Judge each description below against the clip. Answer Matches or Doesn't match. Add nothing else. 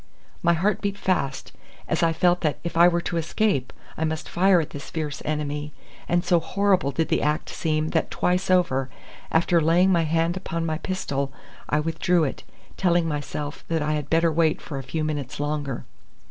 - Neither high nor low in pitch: Matches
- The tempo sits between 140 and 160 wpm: Doesn't match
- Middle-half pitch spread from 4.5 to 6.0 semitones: Doesn't match